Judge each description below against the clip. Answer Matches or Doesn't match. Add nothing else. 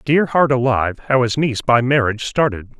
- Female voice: Doesn't match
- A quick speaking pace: Doesn't match